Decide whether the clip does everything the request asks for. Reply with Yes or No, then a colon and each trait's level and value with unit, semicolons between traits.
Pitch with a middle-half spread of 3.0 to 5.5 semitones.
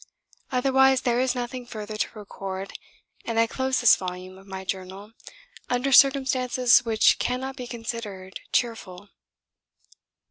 Yes: average, 4.5 semitones